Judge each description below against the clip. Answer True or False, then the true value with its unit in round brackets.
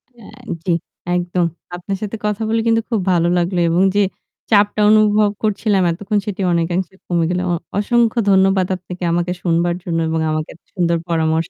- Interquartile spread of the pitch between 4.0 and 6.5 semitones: False (3.3 semitones)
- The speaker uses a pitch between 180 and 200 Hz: True (185 Hz)